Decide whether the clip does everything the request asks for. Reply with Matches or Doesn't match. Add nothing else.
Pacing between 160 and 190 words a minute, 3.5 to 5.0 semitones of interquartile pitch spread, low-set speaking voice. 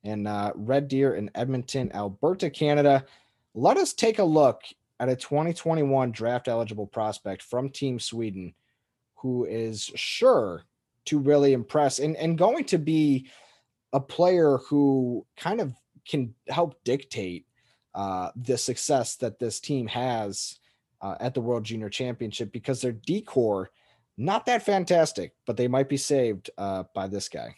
Doesn't match